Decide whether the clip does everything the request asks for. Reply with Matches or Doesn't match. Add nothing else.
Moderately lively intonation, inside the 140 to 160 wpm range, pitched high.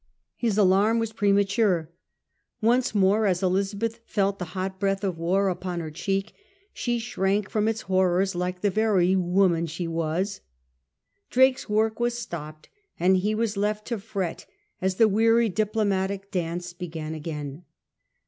Matches